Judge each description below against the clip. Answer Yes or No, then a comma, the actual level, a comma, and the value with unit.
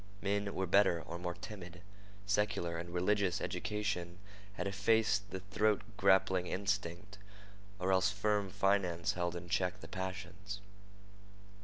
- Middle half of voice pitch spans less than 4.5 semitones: Yes, narrow, 2.4 semitones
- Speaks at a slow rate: Yes, slow, 130 wpm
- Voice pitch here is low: Yes, very low, 95 Hz